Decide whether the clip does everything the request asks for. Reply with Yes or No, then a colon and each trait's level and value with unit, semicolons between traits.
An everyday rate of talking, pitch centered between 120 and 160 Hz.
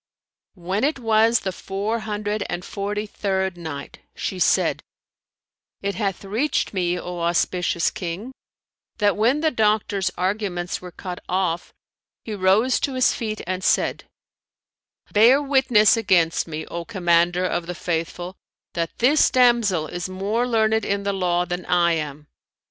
No: average, 145 wpm; high, 195 Hz